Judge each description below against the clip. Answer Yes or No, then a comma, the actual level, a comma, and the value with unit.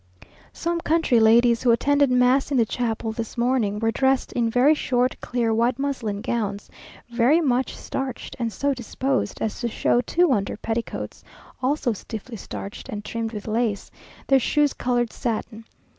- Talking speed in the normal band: Yes, average, 160 wpm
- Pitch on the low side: No, high, 240 Hz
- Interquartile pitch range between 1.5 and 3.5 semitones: Yes, average, 2.9 semitones